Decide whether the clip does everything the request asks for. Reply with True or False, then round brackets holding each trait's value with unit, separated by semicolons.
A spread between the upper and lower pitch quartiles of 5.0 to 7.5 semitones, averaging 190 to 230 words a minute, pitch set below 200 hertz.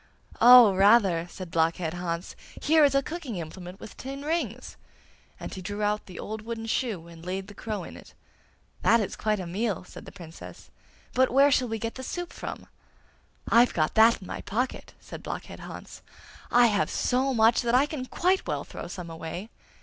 False (5.5 semitones; 195 wpm; 220 Hz)